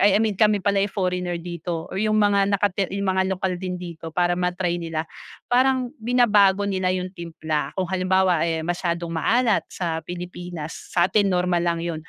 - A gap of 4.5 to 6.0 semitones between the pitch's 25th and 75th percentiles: No, narrow, 2.5 semitones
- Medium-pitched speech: Yes, medium, 180 Hz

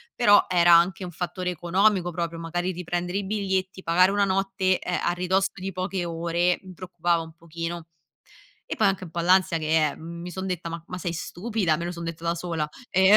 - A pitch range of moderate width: No, narrow, 1.9 semitones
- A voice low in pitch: No, medium, 175 Hz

